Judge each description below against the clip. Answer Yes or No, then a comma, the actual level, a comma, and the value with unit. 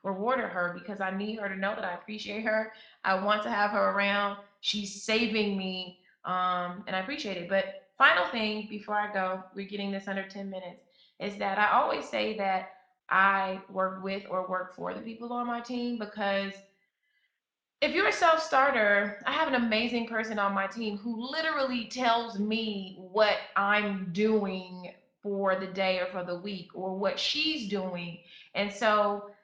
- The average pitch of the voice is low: No, high, 200 Hz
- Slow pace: No, average, 180 wpm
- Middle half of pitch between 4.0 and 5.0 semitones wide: No, narrow, 2.5 semitones